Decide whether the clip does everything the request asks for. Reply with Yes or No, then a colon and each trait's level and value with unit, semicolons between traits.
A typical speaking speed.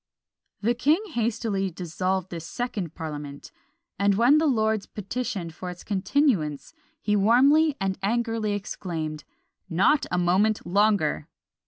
No: slow, 125 wpm